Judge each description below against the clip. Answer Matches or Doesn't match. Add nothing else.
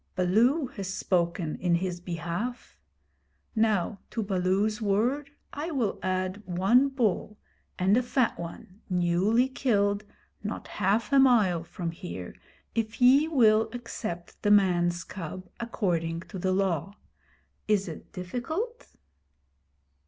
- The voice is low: Doesn't match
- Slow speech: Matches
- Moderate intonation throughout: Matches